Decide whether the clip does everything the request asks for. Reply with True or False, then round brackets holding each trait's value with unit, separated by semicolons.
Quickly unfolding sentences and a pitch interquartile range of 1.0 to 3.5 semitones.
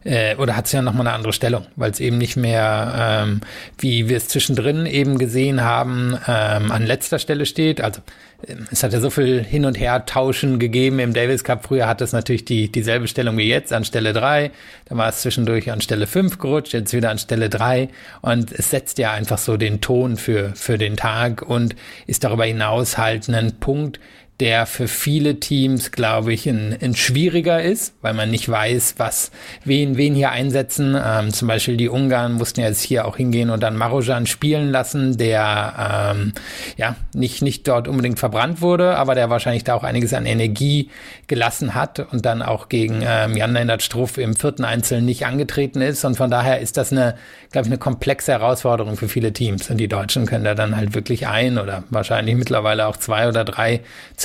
True (200 wpm; 2.9 semitones)